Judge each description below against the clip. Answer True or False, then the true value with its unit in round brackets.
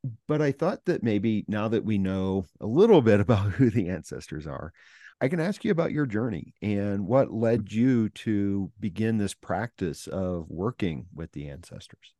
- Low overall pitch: True (110 Hz)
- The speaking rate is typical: True (180 wpm)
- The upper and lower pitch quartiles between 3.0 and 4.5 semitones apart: True (4.2 semitones)